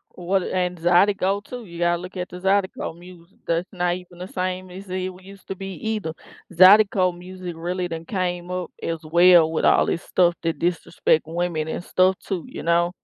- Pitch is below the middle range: No, medium, 180 Hz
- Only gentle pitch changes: Yes, narrow, 1.4 semitones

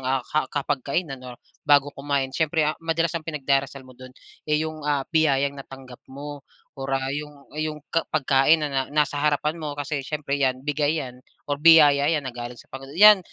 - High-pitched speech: No, medium, 145 Hz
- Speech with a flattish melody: Yes, narrow, 2.1 semitones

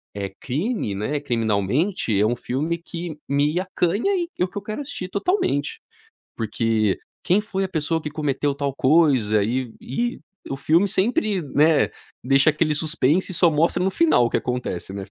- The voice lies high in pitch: No, medium, 150 Hz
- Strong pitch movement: Yes, wide, 6.6 semitones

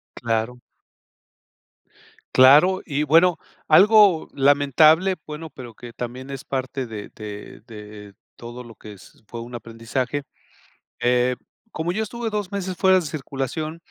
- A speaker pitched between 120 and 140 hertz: Yes, low, 135 Hz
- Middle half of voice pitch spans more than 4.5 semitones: Yes, wide, 5.6 semitones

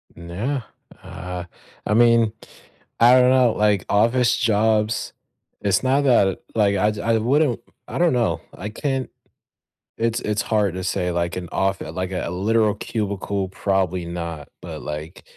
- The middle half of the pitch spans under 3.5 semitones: No, average, 4.2 semitones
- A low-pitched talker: Yes, low, 105 Hz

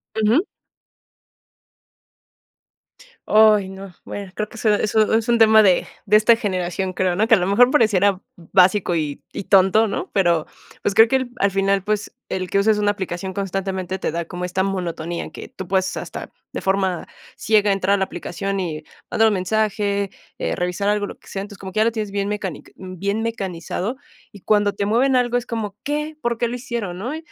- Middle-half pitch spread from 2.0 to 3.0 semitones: Yes, narrow, 2.6 semitones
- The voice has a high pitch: Yes, high, 200 Hz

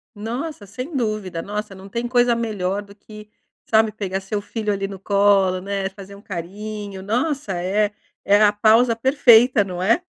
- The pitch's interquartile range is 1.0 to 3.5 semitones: Yes, narrow, 2.6 semitones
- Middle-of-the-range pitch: No, high, 210 Hz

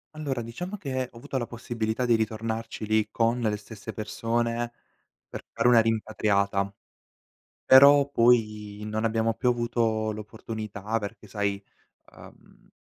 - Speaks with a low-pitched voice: Yes, low, 115 Hz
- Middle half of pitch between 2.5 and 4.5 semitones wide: No, narrow, 1.8 semitones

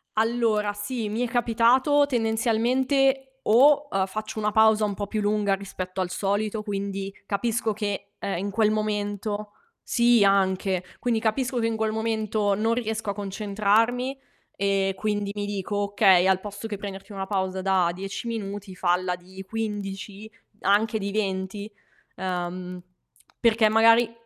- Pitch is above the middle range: Yes, high, 210 Hz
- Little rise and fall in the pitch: Yes, narrow, 2.3 semitones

